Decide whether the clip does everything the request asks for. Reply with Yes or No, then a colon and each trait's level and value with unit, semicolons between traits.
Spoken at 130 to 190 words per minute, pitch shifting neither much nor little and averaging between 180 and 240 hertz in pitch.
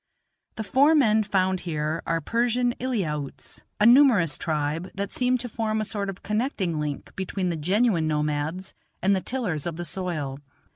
No: average, 165 wpm; wide, 6.2 semitones; high, 190 Hz